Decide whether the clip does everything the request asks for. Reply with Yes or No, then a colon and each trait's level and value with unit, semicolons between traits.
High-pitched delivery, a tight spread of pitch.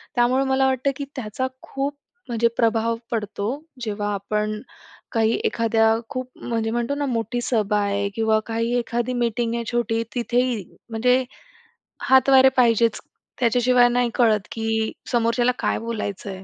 Yes: high, 235 Hz; narrow, 2.0 semitones